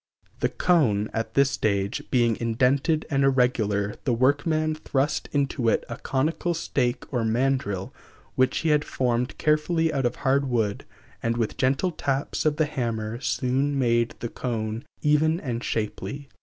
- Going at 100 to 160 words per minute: Yes, average, 155 wpm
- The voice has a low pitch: Yes, low, 130 Hz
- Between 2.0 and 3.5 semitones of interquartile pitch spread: No, average, 3.9 semitones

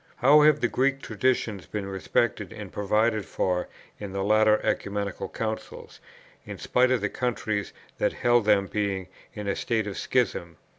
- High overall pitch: No, low, 105 Hz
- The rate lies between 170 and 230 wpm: No, average, 160 wpm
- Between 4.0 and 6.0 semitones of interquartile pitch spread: No, average, 3.4 semitones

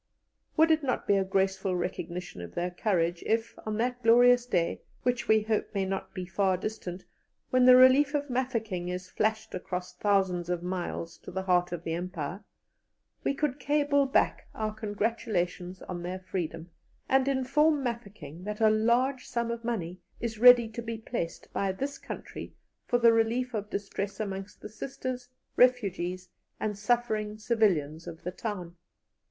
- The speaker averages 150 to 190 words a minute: Yes, average, 165 wpm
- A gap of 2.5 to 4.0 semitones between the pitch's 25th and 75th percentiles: No, average, 5.0 semitones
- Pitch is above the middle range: Yes, high, 210 Hz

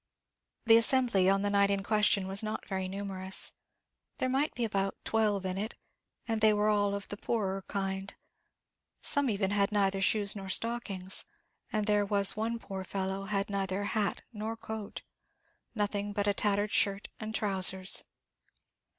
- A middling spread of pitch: No, narrow, 1.8 semitones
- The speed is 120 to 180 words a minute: Yes, average, 160 wpm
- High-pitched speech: Yes, high, 200 Hz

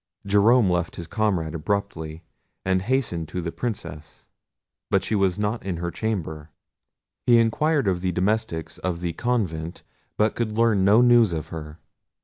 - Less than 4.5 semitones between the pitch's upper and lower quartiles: No, average, 4.9 semitones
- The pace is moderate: Yes, average, 155 wpm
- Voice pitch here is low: Yes, very low, 95 Hz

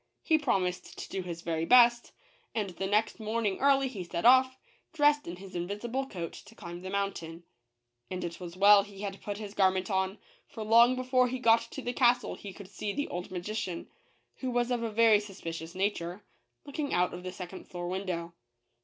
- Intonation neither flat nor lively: Yes, average, 4.8 semitones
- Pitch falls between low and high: No, high, 200 Hz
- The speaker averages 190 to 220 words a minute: Yes, average, 200 wpm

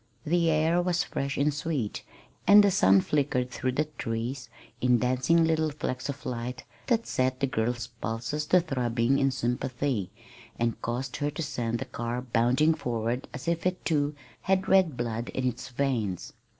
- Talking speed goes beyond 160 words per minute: Yes, average, 170 wpm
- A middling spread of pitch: Yes, average, 4.3 semitones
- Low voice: Yes, low, 130 Hz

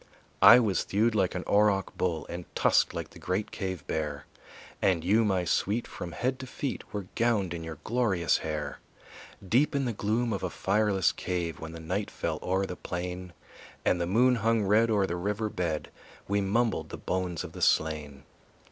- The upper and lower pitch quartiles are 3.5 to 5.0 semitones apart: Yes, average, 3.9 semitones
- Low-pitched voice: Yes, very low, 95 Hz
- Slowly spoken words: No, average, 190 wpm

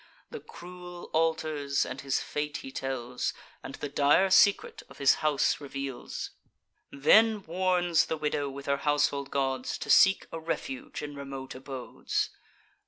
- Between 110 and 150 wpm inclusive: Yes, average, 145 wpm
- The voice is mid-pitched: Yes, medium, 145 Hz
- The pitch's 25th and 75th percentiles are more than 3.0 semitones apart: Yes, average, 4.2 semitones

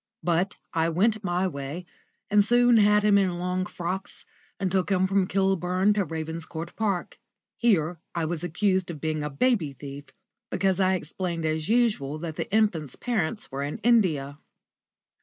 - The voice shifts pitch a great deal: No, average, 4.0 semitones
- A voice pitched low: No, medium, 180 Hz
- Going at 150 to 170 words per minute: Yes, average, 160 wpm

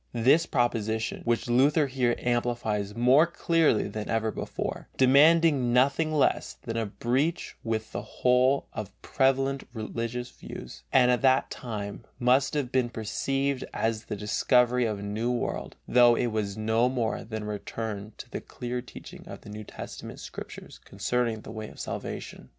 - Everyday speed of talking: Yes, average, 160 wpm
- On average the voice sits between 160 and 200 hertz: No, low, 120 Hz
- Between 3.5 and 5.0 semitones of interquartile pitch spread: No, average, 3.1 semitones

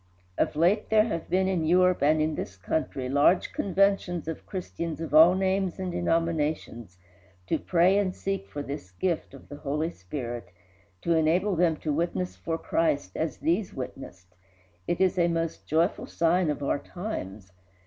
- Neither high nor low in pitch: Yes, medium, 165 Hz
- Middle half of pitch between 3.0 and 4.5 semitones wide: Yes, average, 4.1 semitones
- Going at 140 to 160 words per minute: No, average, 170 wpm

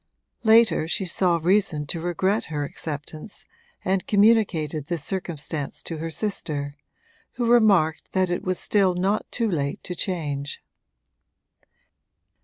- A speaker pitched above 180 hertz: No, medium, 175 Hz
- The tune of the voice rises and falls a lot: No, average, 4.5 semitones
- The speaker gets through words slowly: Yes, slow, 125 wpm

